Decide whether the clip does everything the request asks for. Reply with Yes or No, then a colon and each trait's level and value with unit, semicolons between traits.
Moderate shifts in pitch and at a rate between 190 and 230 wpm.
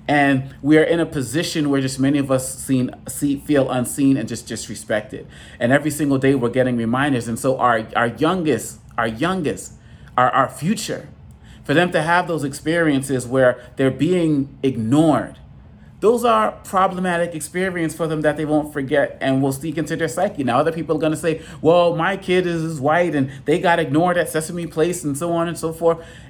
Yes: average, 3.6 semitones; average, 195 wpm